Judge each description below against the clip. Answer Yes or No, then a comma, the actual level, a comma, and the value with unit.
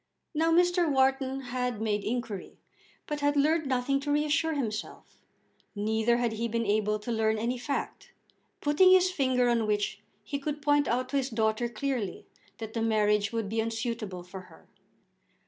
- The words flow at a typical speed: Yes, average, 165 wpm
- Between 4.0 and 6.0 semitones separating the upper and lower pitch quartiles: Yes, average, 4.5 semitones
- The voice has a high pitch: Yes, high, 240 Hz